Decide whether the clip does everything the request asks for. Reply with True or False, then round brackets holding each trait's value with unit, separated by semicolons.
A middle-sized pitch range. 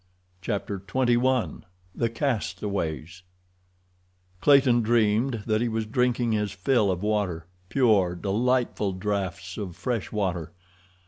True (3.8 semitones)